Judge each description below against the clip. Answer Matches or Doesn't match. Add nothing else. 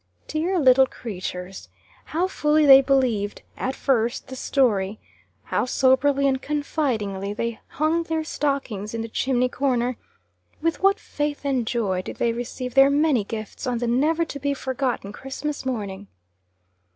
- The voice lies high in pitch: Matches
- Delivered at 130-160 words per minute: Matches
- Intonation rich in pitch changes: Doesn't match